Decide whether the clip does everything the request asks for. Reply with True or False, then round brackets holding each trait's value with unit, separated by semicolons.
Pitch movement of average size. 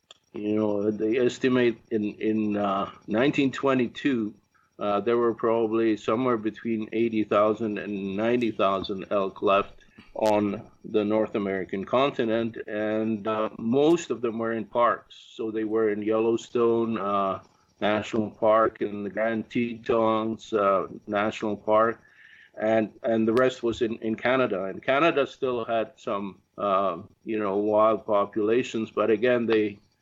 False (1.4 semitones)